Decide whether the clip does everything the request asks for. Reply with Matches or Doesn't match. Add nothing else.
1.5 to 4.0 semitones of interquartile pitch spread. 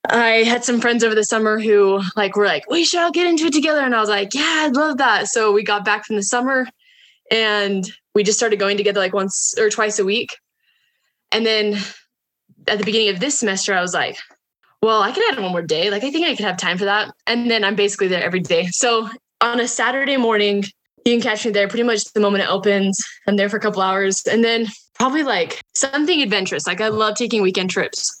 Matches